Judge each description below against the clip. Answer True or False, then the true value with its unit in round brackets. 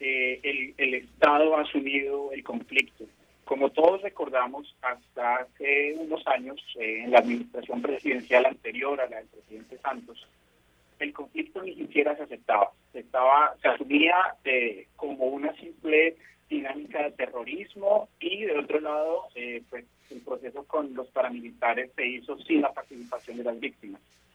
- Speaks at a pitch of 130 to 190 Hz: True (140 Hz)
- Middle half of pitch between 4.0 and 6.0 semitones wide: True (4.3 semitones)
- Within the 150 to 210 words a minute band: True (155 wpm)